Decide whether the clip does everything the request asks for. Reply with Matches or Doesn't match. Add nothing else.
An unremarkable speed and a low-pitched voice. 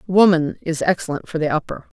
Doesn't match